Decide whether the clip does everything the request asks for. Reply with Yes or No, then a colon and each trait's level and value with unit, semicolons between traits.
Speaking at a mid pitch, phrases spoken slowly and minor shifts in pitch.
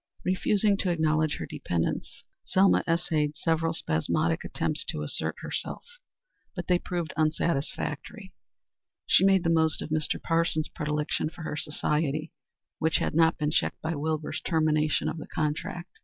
No: medium, 160 Hz; average, 145 wpm; narrow, 2.1 semitones